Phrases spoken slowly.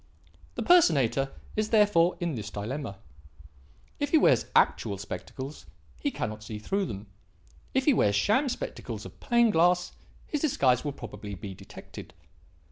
No: average, 145 wpm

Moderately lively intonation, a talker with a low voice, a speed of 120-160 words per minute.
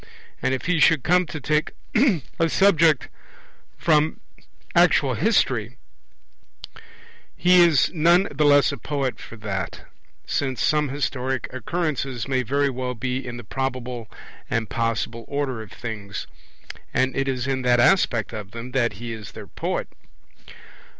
Yes: average, 4.2 semitones; low, 130 Hz; average, 145 wpm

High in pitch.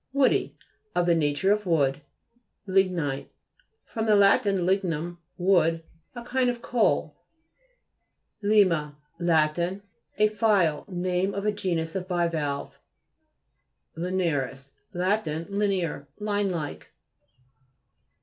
No: medium, 180 Hz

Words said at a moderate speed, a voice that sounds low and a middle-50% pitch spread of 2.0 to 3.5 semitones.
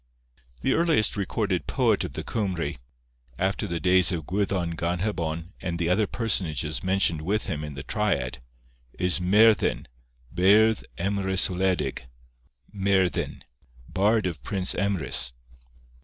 No: slow, 125 wpm; very low, 95 Hz; average, 3.0 semitones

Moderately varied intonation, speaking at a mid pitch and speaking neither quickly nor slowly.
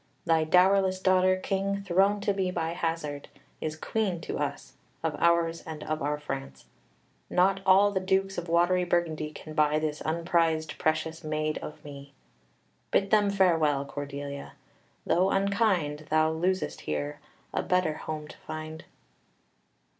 Yes: average, 3.4 semitones; medium, 165 Hz; average, 145 wpm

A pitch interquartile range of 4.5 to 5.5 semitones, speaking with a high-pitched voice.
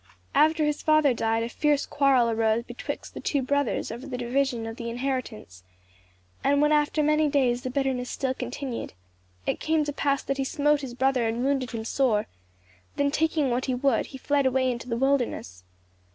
No: average, 3.0 semitones; very high, 265 Hz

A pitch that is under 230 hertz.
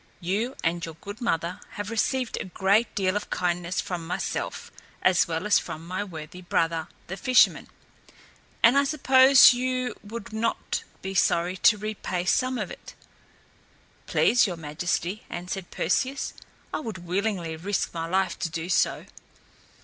Yes: high, 190 Hz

